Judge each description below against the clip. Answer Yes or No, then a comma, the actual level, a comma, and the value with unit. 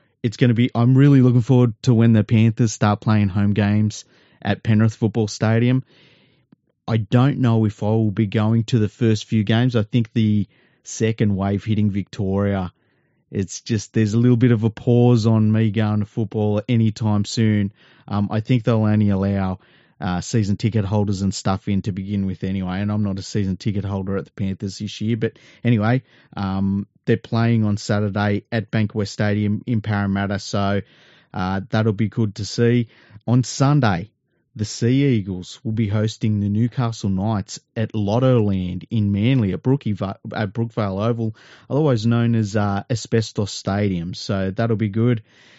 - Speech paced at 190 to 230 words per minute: No, average, 180 wpm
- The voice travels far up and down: No, narrow, 2.4 semitones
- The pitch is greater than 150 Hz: No, low, 110 Hz